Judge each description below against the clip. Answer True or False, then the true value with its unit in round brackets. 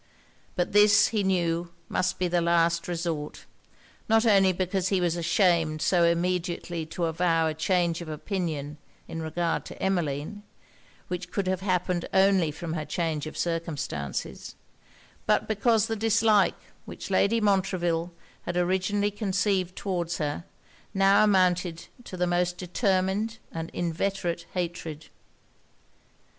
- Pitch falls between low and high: True (180 Hz)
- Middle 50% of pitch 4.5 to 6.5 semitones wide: False (2.5 semitones)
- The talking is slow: True (130 wpm)